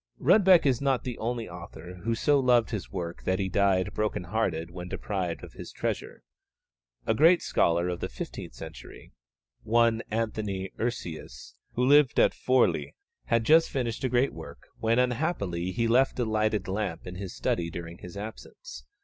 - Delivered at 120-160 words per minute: No, average, 170 wpm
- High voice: No, low, 110 Hz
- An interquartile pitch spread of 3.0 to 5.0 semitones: No, wide, 5.4 semitones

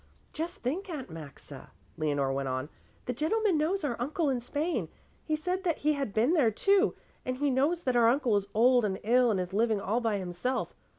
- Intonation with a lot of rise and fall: Yes, wide, 7.2 semitones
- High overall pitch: Yes, very high, 250 Hz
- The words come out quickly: Yes, fast, 210 wpm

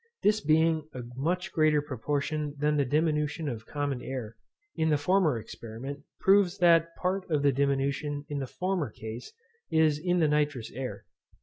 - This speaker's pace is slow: No, average, 165 wpm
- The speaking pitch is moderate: Yes, medium, 150 Hz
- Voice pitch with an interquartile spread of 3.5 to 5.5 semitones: No, average, 3.1 semitones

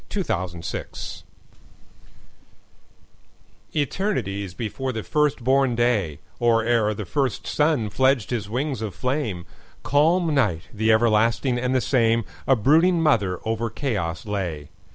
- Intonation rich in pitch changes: No, average, 4.8 semitones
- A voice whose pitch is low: Yes, low, 115 Hz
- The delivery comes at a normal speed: No, slow, 110 wpm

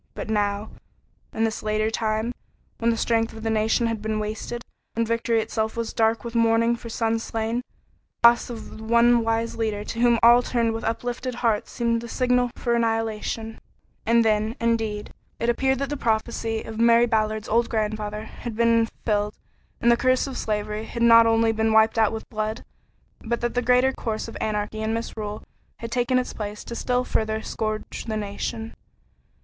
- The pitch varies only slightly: Yes, narrow, 1.3 semitones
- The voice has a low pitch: No, high, 225 Hz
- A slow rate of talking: No, average, 190 wpm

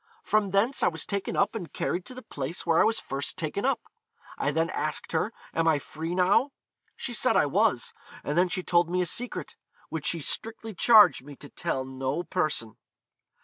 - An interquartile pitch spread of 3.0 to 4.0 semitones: No, wide, 5.6 semitones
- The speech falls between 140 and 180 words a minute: No, average, 200 wpm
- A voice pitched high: No, medium, 175 Hz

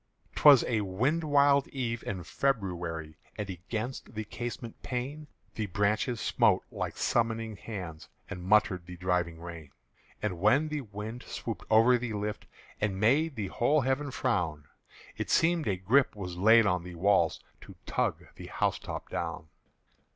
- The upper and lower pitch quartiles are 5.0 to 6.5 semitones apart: Yes, wide, 5.6 semitones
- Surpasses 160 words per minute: No, average, 155 wpm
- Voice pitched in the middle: No, low, 110 Hz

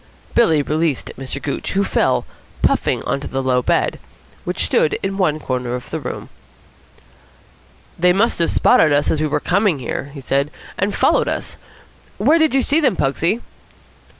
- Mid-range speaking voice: Yes, medium, 155 Hz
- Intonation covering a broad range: Yes, wide, 6.0 semitones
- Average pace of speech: Yes, average, 175 wpm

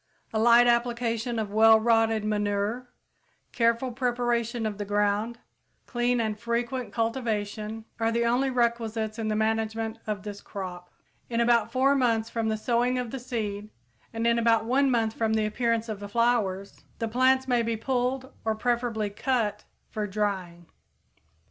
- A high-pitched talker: Yes, high, 230 Hz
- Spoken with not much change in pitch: Yes, narrow, 2.0 semitones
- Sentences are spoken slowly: No, average, 160 wpm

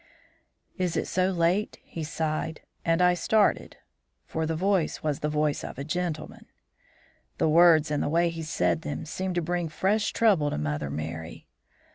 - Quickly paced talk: No, average, 170 wpm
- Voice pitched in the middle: Yes, medium, 160 Hz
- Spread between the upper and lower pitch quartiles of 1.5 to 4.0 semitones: Yes, average, 3.0 semitones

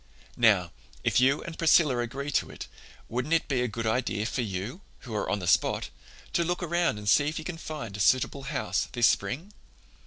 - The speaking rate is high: Yes, fast, 210 wpm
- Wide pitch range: Yes, wide, 6.2 semitones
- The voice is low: Yes, low, 125 Hz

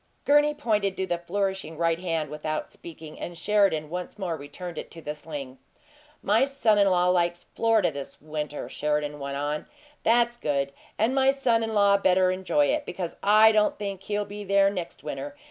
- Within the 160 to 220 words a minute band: Yes, average, 185 wpm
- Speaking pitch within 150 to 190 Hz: Yes, medium, 185 Hz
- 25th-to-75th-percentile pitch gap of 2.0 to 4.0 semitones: No, average, 5.3 semitones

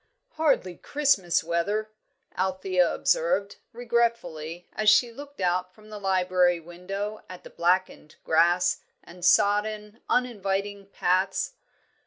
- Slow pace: Yes, slow, 110 wpm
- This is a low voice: No, high, 195 Hz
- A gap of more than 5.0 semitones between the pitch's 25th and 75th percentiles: No, average, 3.2 semitones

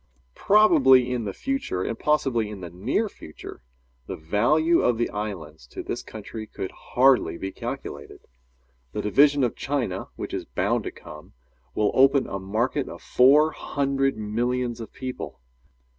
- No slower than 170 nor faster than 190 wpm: No, average, 155 wpm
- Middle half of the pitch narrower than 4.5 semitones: No, average, 4.9 semitones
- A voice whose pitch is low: Yes, low, 120 Hz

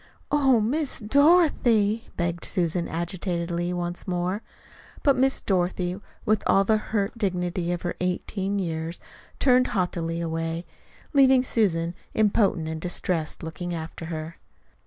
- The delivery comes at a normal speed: No, slow, 125 wpm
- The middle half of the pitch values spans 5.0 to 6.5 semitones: No, average, 4.3 semitones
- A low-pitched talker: No, medium, 180 Hz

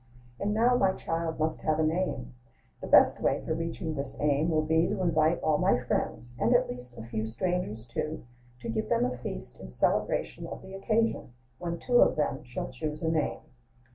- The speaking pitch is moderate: Yes, medium, 155 Hz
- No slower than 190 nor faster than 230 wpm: Yes, average, 200 wpm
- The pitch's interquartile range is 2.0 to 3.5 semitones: No, wide, 5.6 semitones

